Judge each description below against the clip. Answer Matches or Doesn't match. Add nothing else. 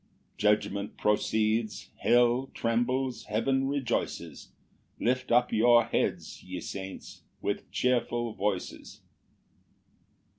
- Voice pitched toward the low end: Matches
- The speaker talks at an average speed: Doesn't match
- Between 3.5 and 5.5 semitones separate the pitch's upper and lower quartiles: Doesn't match